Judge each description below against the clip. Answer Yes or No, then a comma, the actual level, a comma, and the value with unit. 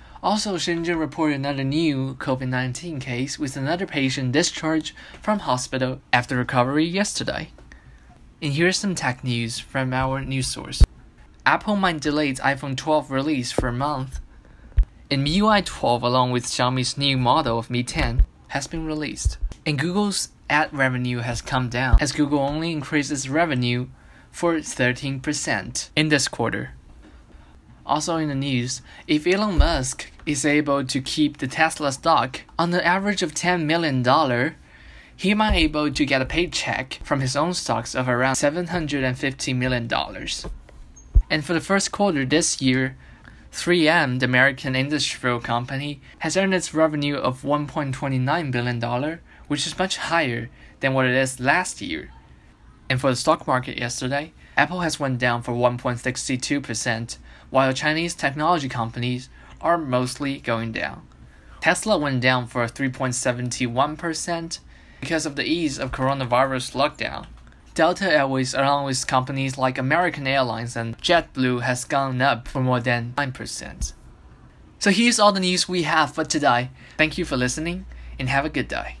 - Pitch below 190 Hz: Yes, low, 135 Hz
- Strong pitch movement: No, average, 3.8 semitones